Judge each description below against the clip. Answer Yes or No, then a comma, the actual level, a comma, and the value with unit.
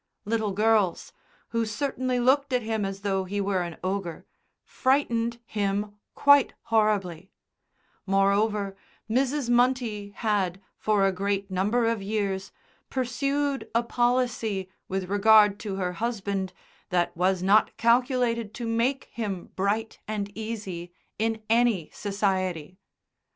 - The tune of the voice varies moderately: Yes, average, 3.3 semitones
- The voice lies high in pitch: Yes, high, 210 Hz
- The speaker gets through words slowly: Yes, slow, 125 wpm